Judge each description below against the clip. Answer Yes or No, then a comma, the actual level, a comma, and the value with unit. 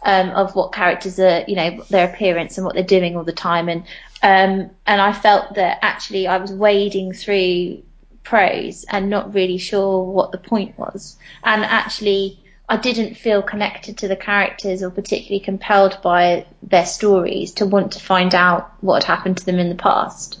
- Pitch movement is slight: Yes, narrow, 1.8 semitones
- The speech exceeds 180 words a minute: Yes, average, 190 wpm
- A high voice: Yes, high, 195 Hz